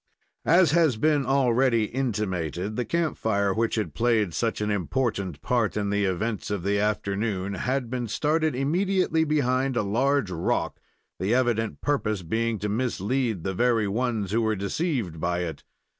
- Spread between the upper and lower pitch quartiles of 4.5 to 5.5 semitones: Yes, average, 4.8 semitones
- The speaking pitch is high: No, low, 115 Hz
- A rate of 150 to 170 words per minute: Yes, average, 160 wpm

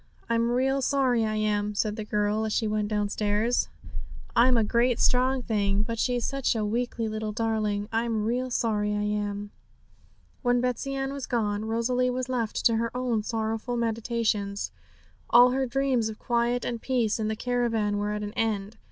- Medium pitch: No, high, 225 Hz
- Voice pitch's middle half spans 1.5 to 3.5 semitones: Yes, narrow, 2.6 semitones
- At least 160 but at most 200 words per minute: Yes, average, 180 wpm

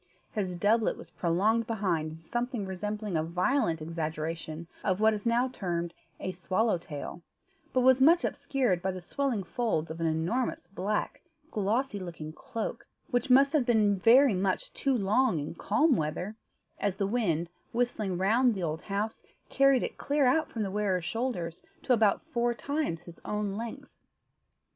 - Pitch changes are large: Yes, wide, 5.8 semitones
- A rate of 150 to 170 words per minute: Yes, average, 165 wpm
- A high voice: Yes, high, 210 Hz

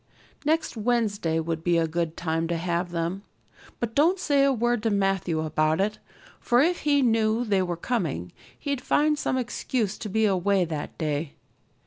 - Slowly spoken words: No, average, 175 wpm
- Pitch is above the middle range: Yes, high, 200 Hz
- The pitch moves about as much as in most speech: No, wide, 6.5 semitones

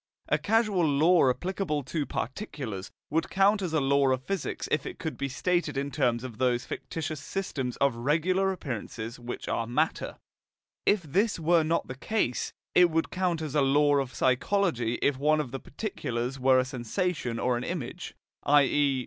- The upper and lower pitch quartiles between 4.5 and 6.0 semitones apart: Yes, average, 5.2 semitones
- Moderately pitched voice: Yes, medium, 145 Hz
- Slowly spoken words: No, average, 175 wpm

